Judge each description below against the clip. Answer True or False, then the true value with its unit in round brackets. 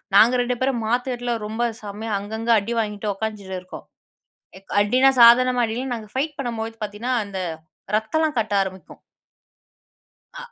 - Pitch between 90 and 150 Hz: False (225 Hz)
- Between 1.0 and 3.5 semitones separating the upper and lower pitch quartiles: True (3.1 semitones)